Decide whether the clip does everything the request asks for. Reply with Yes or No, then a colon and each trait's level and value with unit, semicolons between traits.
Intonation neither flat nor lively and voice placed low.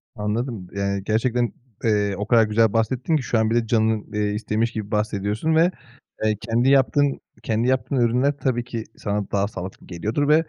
Yes: average, 3.0 semitones; low, 115 Hz